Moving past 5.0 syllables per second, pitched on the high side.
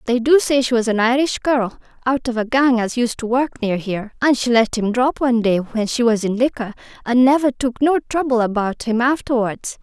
Yes: 5.3 syllables/s; high, 240 Hz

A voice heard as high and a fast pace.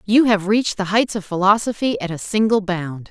Yes: high, 200 Hz; fast, 215 wpm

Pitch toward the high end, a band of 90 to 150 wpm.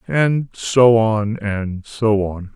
No: low, 110 Hz; average, 140 wpm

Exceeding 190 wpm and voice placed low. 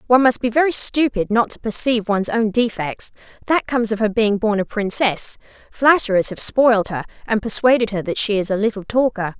No: fast, 205 wpm; high, 225 Hz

